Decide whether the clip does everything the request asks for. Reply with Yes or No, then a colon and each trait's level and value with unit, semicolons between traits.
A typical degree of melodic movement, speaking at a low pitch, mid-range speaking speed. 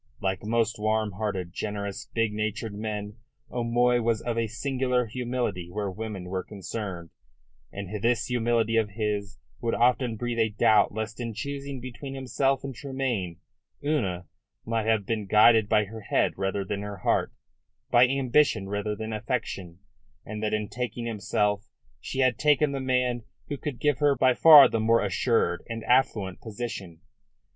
Yes: average, 3.1 semitones; low, 110 Hz; average, 160 wpm